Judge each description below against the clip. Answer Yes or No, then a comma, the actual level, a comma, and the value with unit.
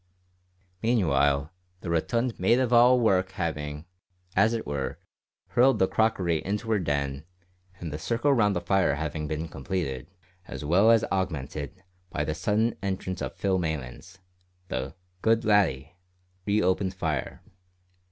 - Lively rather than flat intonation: Yes, wide, 6.4 semitones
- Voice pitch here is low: Yes, very low, 90 Hz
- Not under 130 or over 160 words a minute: Yes, average, 140 wpm